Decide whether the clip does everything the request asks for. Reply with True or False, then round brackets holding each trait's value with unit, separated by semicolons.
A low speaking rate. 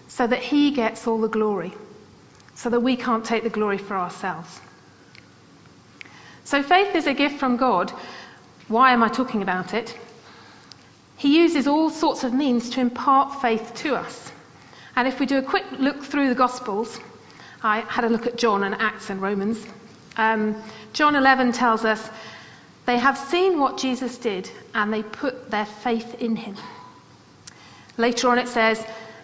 False (170 wpm)